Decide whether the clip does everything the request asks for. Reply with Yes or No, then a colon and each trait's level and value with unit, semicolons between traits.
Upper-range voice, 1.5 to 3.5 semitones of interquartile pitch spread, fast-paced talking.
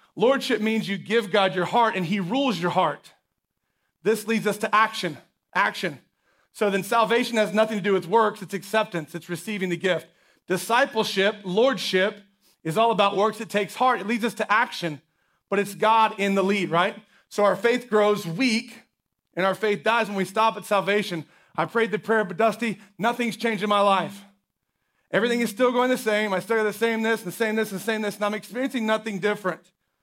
Yes: high, 210 Hz; average, 2.8 semitones; fast, 210 wpm